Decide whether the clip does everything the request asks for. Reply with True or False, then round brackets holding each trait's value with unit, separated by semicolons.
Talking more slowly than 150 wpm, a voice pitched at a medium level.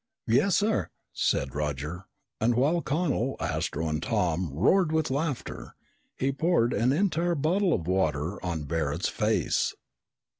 False (135 wpm; 115 Hz)